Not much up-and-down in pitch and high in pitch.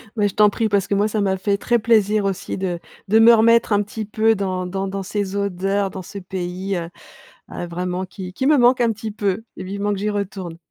Yes: narrow, 2.3 semitones; high, 200 Hz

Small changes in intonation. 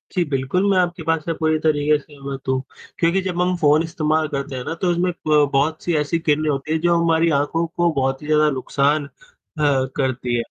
No: average, 3.1 semitones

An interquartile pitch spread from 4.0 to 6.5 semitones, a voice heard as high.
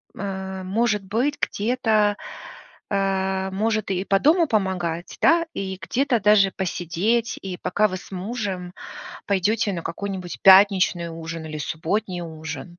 No: average, 3.0 semitones; high, 195 Hz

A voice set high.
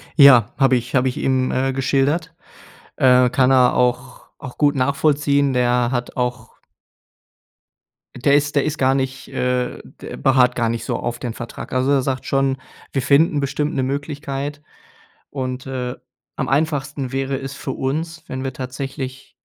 No: low, 135 Hz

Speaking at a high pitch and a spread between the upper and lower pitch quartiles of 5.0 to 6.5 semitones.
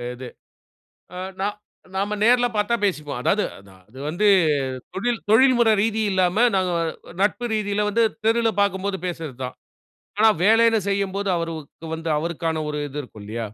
Yes: high, 195 Hz; average, 5.3 semitones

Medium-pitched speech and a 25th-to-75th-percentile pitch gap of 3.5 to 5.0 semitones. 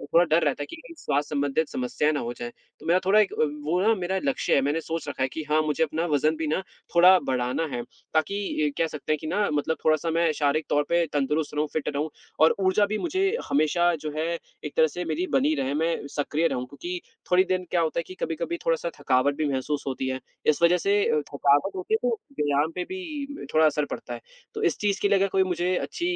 Yes: medium, 160 Hz; average, 4.0 semitones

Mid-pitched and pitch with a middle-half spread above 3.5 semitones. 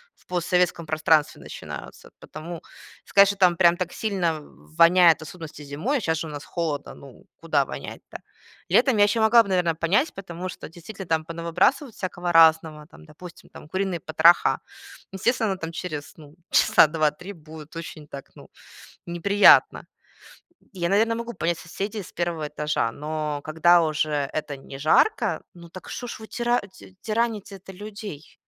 Yes: medium, 170 Hz; average, 3.9 semitones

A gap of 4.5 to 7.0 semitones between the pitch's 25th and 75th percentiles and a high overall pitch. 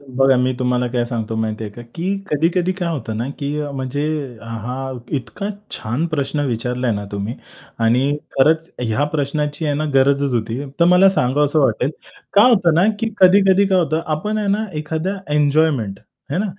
No: average, 4.8 semitones; medium, 140 Hz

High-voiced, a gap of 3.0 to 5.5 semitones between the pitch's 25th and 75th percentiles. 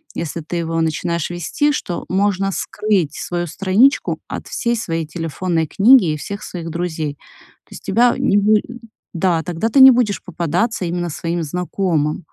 No: medium, 175 Hz; average, 3.6 semitones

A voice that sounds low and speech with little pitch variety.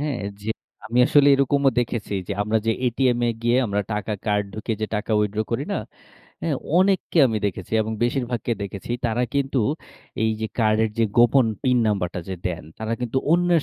No: low, 115 Hz; average, 3.7 semitones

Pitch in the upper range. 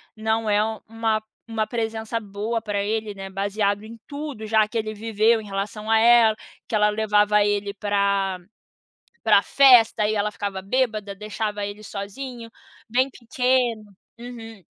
Yes: high, 215 Hz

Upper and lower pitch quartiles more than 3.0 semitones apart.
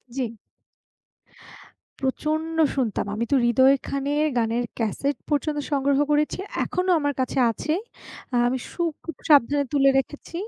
No: narrow, 2.5 semitones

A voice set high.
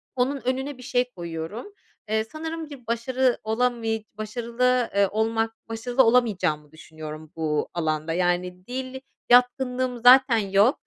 Yes: high, 230 Hz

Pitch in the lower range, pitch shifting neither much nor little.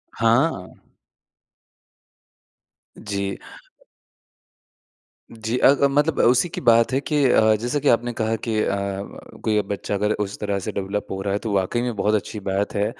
Yes: low, 110 Hz; average, 3.2 semitones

